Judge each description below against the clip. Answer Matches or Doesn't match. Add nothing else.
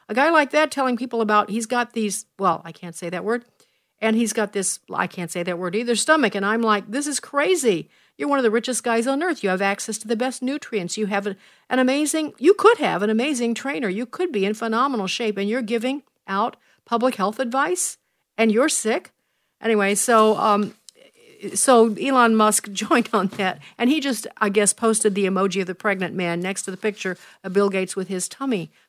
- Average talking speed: Doesn't match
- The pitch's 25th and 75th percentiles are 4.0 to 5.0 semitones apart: Matches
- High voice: Matches